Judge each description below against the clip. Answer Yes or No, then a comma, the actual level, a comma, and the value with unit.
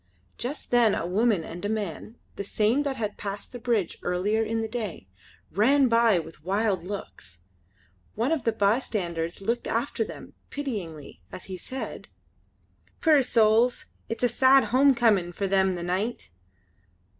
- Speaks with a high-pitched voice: Yes, high, 215 Hz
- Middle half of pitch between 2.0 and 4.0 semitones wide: No, average, 4.4 semitones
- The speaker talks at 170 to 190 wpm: No, average, 155 wpm